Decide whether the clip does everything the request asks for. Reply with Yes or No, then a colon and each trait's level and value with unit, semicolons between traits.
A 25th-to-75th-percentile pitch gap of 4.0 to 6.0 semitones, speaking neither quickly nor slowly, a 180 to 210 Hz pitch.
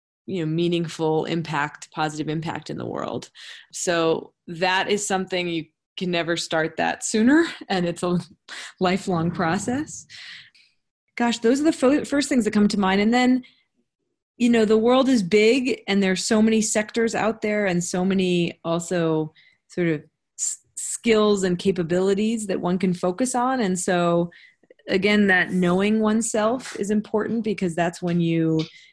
Yes: average, 4.3 semitones; average, 160 wpm; high, 190 Hz